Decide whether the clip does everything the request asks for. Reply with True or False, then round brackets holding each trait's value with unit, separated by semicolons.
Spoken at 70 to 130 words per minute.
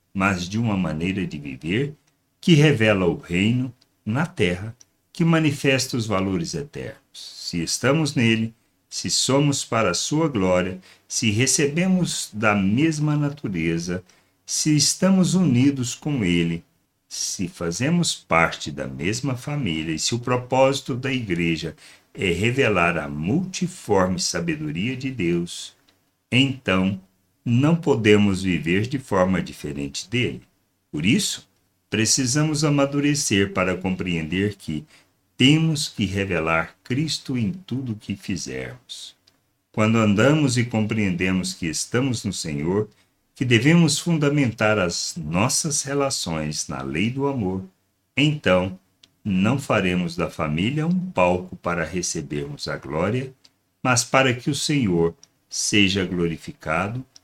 True (120 wpm)